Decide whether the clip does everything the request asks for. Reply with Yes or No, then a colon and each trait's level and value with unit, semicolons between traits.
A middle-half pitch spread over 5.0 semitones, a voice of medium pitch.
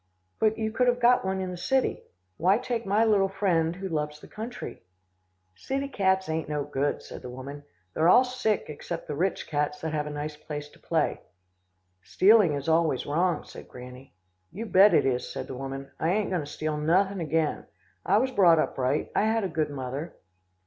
Yes: wide, 5.6 semitones; medium, 165 Hz